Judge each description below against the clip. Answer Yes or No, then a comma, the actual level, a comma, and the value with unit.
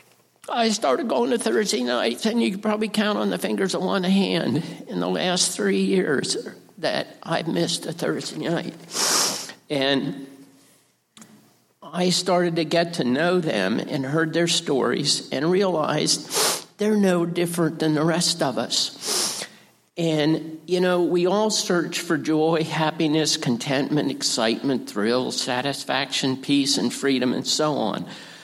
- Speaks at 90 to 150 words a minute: Yes, average, 145 wpm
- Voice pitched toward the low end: No, medium, 170 Hz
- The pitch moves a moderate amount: Yes, average, 3.8 semitones